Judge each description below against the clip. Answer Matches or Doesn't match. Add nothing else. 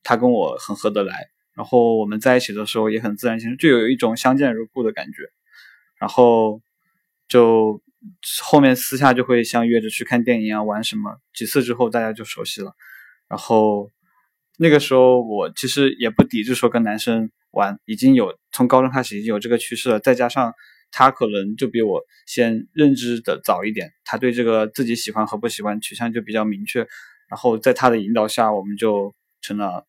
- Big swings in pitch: Doesn't match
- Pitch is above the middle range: Doesn't match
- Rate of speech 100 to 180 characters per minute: Doesn't match